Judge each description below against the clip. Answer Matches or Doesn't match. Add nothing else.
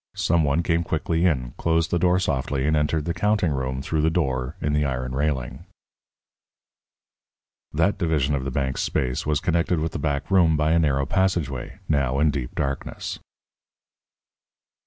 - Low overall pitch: Matches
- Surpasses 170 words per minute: Doesn't match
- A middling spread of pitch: Matches